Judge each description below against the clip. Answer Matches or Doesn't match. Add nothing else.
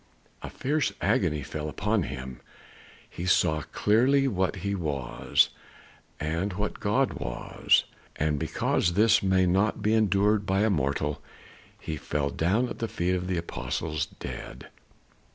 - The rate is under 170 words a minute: Matches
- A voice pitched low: Matches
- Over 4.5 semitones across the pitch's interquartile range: Matches